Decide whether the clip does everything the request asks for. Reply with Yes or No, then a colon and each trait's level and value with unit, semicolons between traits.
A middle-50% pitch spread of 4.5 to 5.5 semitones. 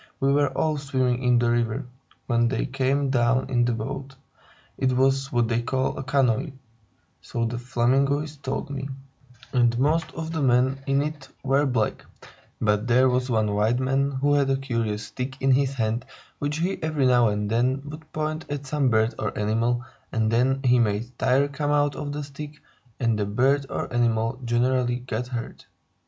No: average, 2.9 semitones